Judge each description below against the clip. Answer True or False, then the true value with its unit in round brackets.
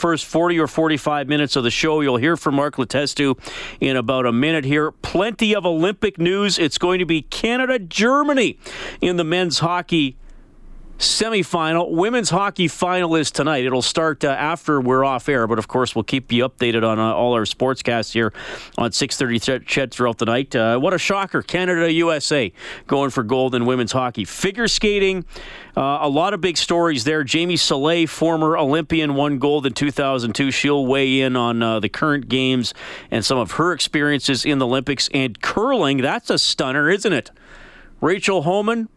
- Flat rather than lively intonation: False (4.8 semitones)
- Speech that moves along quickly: False (185 wpm)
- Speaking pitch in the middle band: True (145 Hz)